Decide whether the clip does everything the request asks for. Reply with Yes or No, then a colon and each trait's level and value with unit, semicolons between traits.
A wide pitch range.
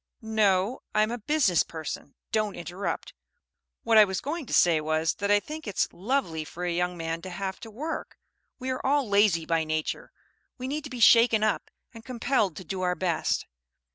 Yes: wide, 5.7 semitones